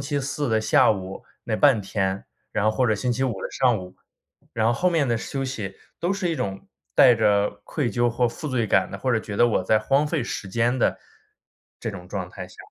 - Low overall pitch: Yes, low, 115 Hz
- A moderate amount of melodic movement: Yes, average, 4.5 semitones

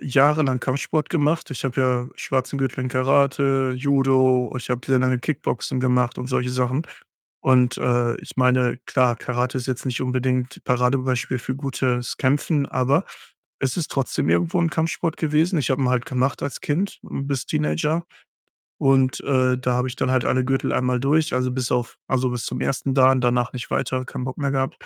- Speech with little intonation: Yes, narrow, 1.6 semitones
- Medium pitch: No, low, 130 Hz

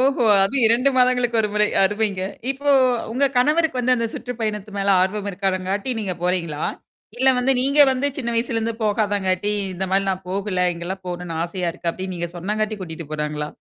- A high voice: Yes, high, 205 Hz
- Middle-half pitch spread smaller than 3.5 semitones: No, average, 4.7 semitones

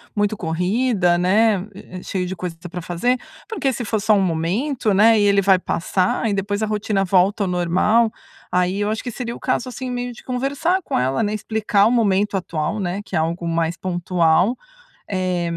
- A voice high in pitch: Yes, high, 200 Hz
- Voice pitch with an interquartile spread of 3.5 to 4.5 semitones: Yes, average, 3.8 semitones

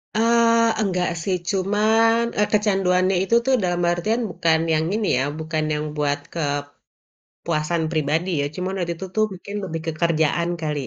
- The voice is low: No, medium, 180 Hz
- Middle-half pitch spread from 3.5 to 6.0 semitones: Yes, average, 4.7 semitones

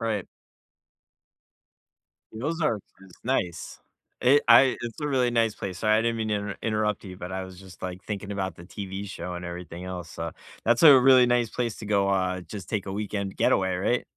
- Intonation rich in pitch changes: No, average, 3.9 semitones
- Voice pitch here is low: Yes, low, 100 Hz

